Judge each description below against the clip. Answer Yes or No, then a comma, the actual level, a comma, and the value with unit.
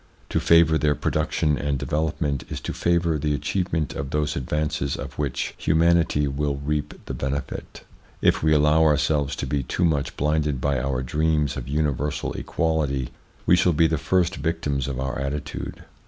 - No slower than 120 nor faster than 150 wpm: No, average, 170 wpm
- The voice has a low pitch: Yes, very low, 75 Hz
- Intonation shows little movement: Yes, narrow, 2.3 semitones